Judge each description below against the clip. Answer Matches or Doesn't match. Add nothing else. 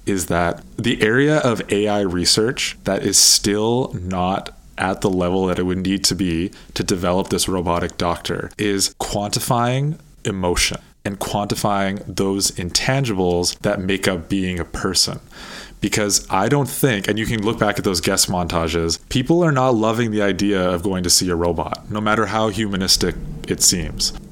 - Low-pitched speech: Matches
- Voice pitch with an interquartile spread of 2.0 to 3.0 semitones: Doesn't match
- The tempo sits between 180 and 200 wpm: Doesn't match